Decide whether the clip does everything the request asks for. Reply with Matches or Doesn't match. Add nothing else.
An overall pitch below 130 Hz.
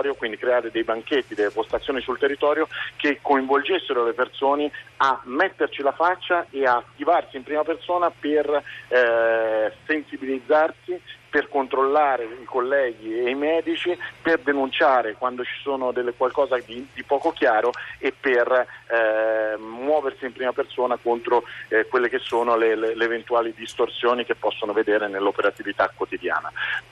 Doesn't match